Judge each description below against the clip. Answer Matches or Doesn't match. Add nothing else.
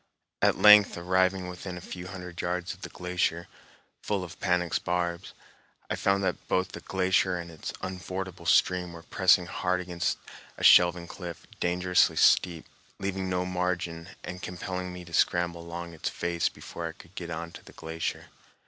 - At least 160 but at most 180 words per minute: Matches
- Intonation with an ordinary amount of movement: Doesn't match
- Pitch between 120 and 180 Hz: Doesn't match